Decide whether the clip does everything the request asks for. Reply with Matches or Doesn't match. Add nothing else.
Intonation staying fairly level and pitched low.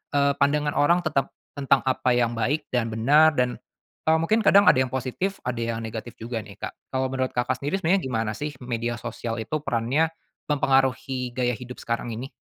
Doesn't match